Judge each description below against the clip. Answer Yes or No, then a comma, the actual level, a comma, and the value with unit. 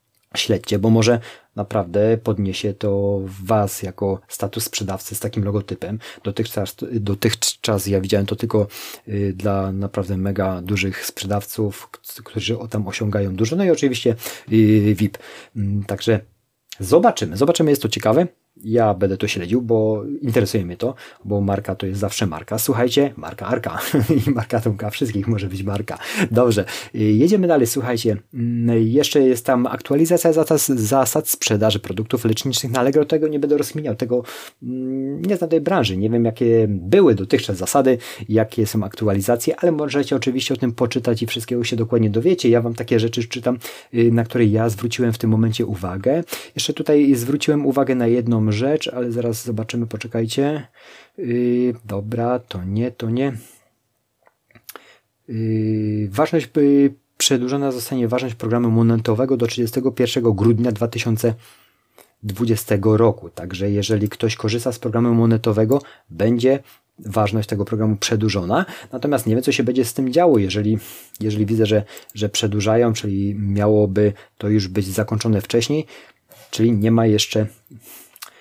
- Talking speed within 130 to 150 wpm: Yes, average, 145 wpm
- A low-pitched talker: Yes, low, 115 Hz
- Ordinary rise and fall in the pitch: Yes, average, 3.2 semitones